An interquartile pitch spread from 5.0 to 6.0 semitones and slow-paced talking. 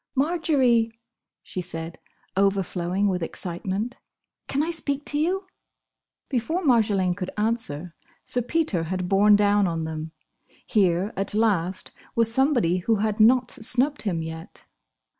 Yes: wide, 5.6 semitones; slow, 130 wpm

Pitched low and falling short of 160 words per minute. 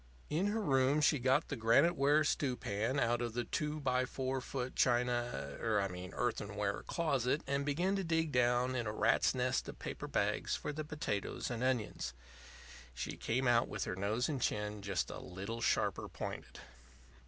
No: low, 125 Hz; average, 175 wpm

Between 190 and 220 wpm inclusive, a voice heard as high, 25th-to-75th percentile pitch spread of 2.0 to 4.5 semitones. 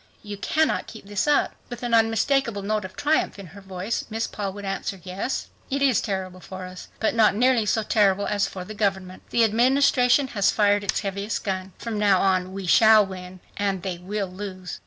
Yes: average, 200 wpm; high, 205 Hz; average, 2.9 semitones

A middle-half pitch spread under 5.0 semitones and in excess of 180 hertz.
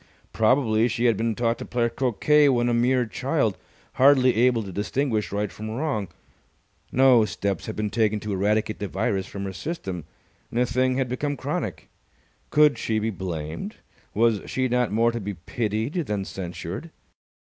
No: average, 3.5 semitones; low, 115 Hz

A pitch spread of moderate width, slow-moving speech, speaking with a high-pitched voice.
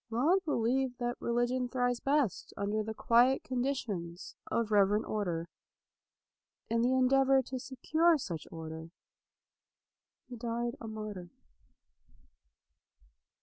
Yes: average, 3.6 semitones; slow, 110 wpm; high, 240 Hz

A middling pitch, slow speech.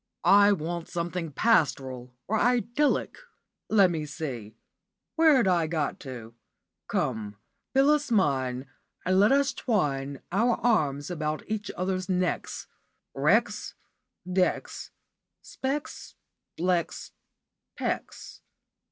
Yes: medium, 180 Hz; slow, 100 wpm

